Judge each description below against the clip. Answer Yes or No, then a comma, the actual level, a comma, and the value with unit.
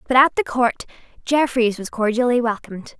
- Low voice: No, high, 240 Hz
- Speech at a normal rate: Yes, average, 160 wpm